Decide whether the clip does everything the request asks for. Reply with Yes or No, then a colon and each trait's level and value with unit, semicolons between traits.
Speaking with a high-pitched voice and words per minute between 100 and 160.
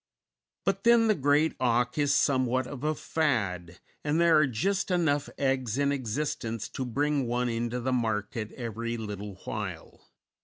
No: low, 130 Hz; average, 155 wpm